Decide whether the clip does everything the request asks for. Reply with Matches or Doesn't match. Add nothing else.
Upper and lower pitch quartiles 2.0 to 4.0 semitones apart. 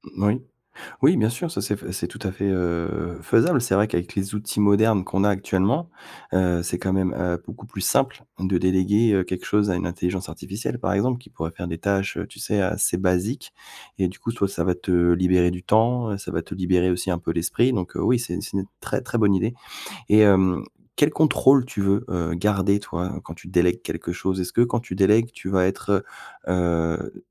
Matches